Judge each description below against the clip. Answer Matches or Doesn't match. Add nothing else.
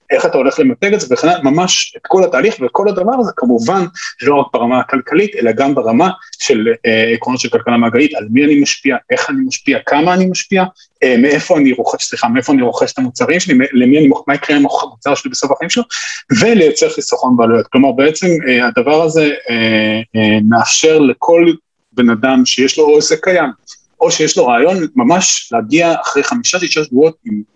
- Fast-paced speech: Matches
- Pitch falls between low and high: Matches